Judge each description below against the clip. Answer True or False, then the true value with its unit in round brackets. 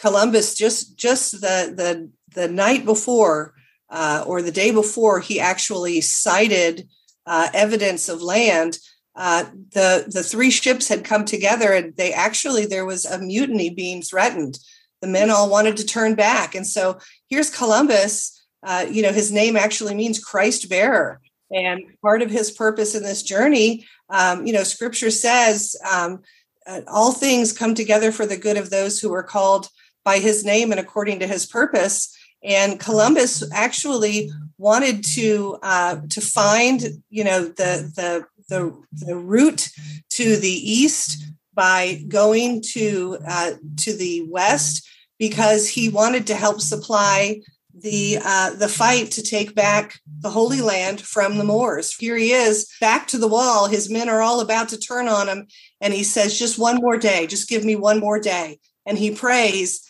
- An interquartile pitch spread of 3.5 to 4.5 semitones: False (3.0 semitones)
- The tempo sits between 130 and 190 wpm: True (170 wpm)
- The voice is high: True (210 Hz)